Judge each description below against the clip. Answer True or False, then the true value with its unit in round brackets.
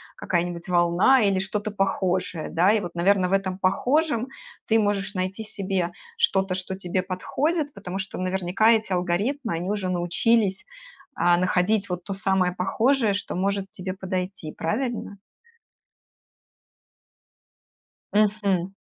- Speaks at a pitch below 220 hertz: True (190 Hz)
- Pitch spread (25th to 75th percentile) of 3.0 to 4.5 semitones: False (2.5 semitones)